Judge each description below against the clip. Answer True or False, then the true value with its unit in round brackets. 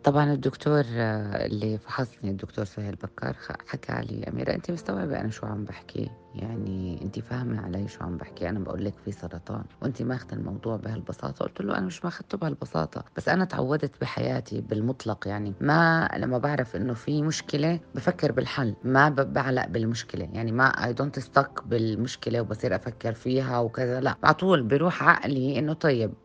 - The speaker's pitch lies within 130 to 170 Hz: False (120 Hz)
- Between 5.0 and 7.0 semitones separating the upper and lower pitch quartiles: True (5.3 semitones)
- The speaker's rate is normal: False (165 wpm)